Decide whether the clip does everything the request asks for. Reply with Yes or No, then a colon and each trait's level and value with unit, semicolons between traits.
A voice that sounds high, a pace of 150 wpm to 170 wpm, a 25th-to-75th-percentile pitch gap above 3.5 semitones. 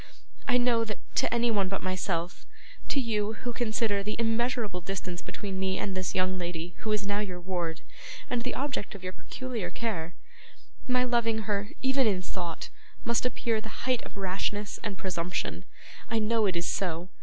No: high, 205 Hz; average, 180 wpm; average, 3.9 semitones